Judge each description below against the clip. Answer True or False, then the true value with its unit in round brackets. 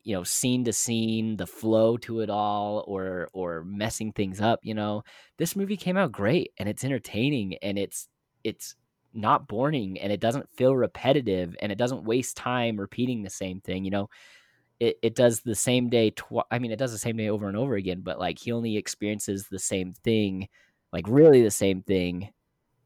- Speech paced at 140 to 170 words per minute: False (200 wpm)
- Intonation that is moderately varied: True (3.4 semitones)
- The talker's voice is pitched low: True (110 Hz)